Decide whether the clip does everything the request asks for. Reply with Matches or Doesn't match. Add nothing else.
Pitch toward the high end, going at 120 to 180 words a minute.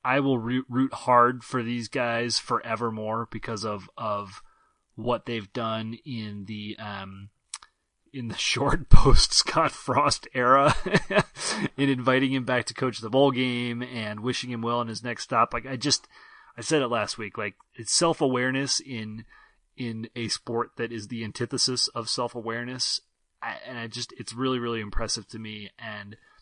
Doesn't match